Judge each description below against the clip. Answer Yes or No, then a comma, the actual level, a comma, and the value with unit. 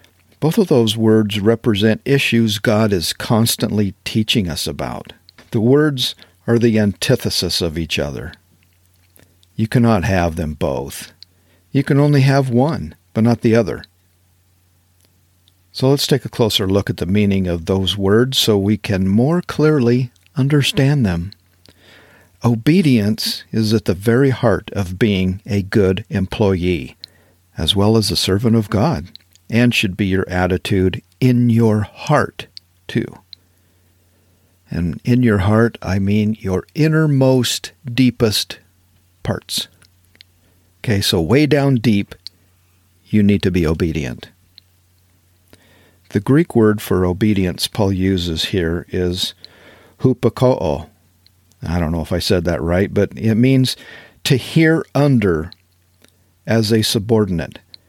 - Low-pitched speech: Yes, low, 100 Hz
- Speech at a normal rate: No, slow, 130 wpm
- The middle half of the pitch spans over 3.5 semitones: Yes, average, 4.4 semitones